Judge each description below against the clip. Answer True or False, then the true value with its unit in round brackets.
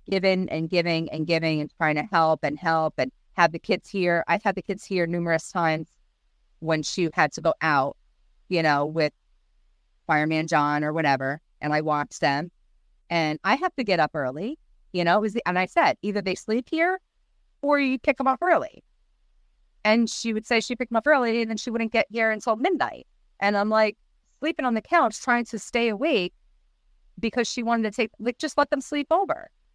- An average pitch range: False (7.1 semitones)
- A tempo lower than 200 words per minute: False (205 wpm)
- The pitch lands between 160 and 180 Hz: False (190 Hz)